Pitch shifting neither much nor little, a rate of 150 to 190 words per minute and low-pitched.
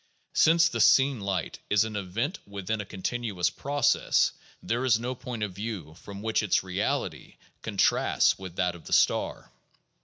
Yes: average, 4.4 semitones; average, 160 wpm; low, 105 Hz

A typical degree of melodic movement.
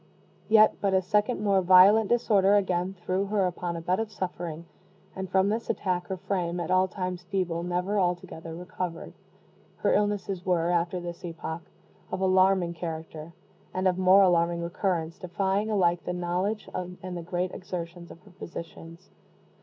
No: narrow, 1.9 semitones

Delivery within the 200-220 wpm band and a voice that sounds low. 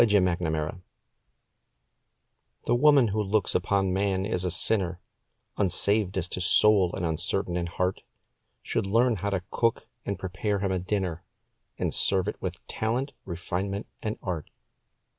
No: average, 145 wpm; very low, 95 Hz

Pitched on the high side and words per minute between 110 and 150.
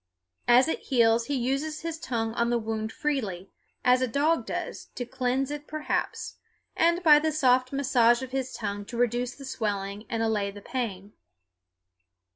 No: very high, 250 Hz; average, 170 wpm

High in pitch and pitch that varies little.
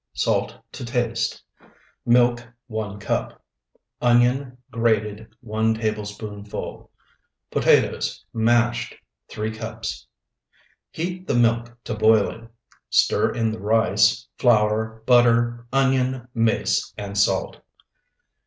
No: low, 115 Hz; narrow, 1.8 semitones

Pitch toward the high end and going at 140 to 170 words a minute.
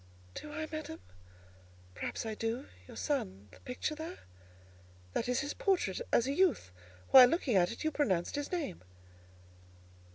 Yes: very high, 250 Hz; average, 150 wpm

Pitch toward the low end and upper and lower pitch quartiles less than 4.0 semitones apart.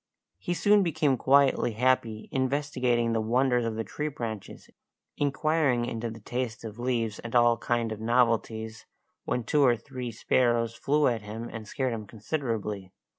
Yes: low, 120 Hz; average, 2.8 semitones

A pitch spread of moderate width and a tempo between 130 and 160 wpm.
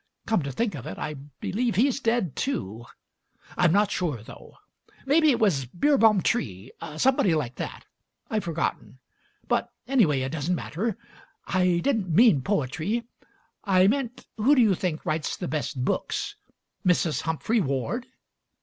No: wide, 7.5 semitones; average, 150 wpm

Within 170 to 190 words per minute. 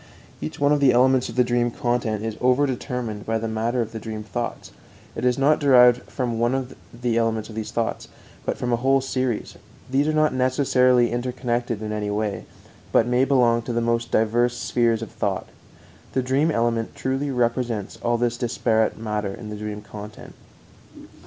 Yes: average, 180 wpm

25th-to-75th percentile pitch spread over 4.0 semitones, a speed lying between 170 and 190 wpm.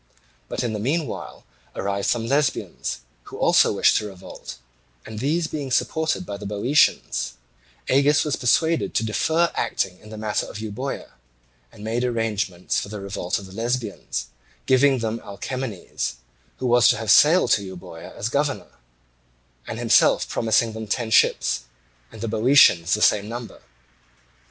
No: average, 4.4 semitones; average, 155 wpm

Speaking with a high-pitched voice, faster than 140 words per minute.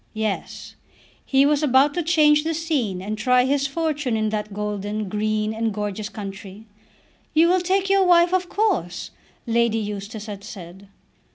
Yes: high, 225 Hz; average, 160 wpm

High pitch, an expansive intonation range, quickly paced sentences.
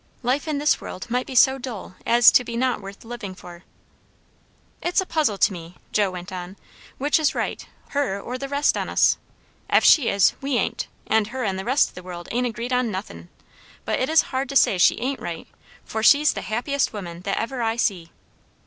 Yes: high, 235 Hz; wide, 5.7 semitones; fast, 215 wpm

